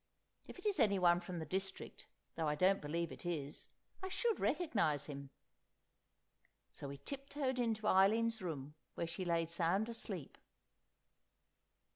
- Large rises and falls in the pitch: Yes, wide, 5.8 semitones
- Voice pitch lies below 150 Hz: No, medium, 185 Hz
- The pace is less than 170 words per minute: Yes, slow, 135 wpm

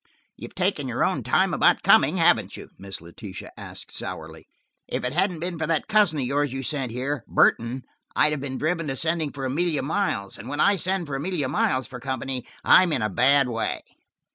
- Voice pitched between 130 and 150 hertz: Yes, medium, 140 Hz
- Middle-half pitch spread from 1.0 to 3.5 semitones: No, average, 4.4 semitones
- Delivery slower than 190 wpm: No, fast, 205 wpm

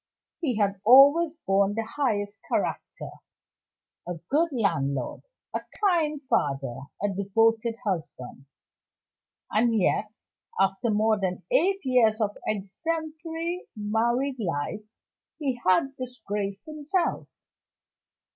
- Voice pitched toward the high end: Yes, high, 225 Hz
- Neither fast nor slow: No, slow, 100 wpm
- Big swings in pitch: Yes, wide, 6.4 semitones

